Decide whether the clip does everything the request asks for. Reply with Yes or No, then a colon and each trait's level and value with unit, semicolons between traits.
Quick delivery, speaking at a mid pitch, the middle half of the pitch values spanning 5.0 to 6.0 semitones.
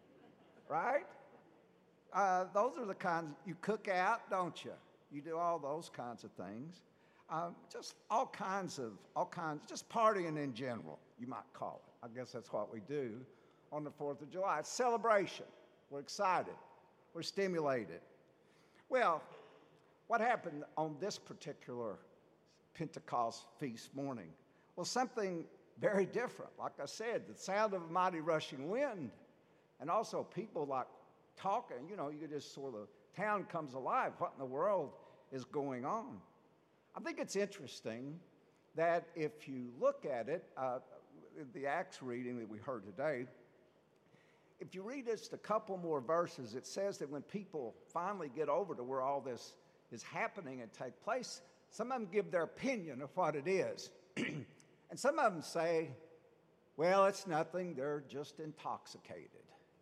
No: average, 160 wpm; medium, 160 Hz; average, 5.3 semitones